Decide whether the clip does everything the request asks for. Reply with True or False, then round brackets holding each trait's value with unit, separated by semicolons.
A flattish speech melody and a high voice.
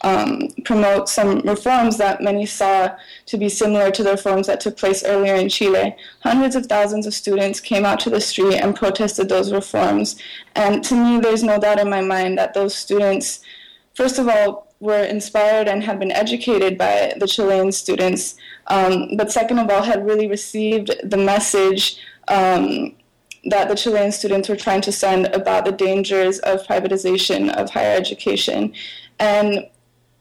True (1.7 semitones; 205 Hz)